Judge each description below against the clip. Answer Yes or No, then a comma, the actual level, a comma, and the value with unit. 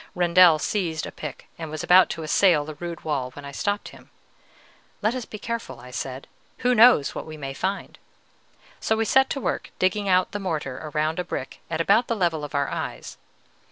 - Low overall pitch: No, medium, 170 Hz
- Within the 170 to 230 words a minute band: Yes, fast, 205 wpm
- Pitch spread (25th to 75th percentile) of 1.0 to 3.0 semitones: No, average, 5.2 semitones